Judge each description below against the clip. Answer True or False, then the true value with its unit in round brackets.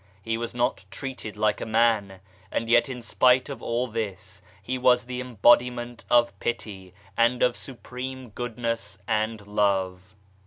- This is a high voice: False (115 Hz)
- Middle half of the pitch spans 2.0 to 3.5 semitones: True (2.9 semitones)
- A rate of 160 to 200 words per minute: False (150 wpm)